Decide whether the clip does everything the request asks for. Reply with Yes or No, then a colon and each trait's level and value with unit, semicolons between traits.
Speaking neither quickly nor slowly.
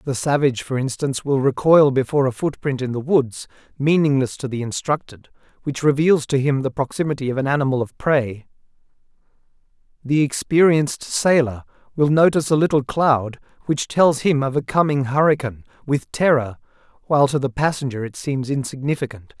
Yes: average, 160 wpm